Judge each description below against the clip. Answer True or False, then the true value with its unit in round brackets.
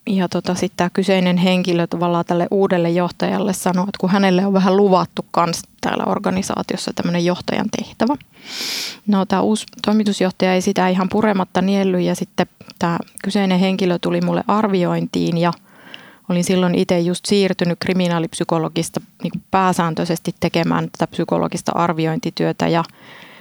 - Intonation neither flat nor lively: False (2.0 semitones)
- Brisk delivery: False (140 wpm)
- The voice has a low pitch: False (185 Hz)